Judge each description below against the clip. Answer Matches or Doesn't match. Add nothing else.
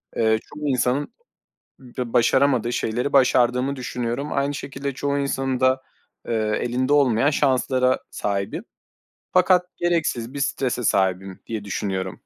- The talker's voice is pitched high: Doesn't match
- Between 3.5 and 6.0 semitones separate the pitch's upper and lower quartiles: Doesn't match